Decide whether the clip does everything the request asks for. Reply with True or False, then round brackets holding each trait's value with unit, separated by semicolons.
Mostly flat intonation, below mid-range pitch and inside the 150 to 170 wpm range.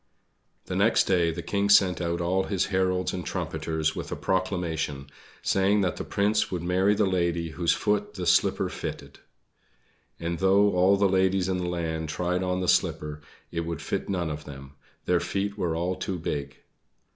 False (2.2 semitones; 90 Hz; 180 wpm)